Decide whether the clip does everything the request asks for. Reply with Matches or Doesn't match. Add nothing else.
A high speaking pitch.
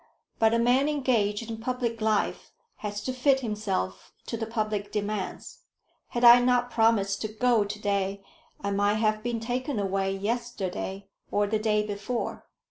Matches